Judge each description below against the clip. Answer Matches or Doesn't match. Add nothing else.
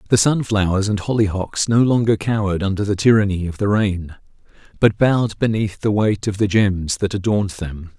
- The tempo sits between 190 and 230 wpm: Doesn't match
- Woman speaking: Doesn't match